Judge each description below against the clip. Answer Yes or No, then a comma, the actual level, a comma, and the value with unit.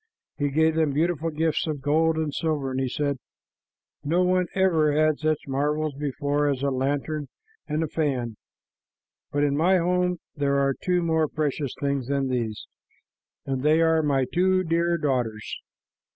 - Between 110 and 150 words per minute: No, average, 165 wpm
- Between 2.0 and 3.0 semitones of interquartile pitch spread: Yes, narrow, 2.6 semitones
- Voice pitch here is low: No, medium, 150 Hz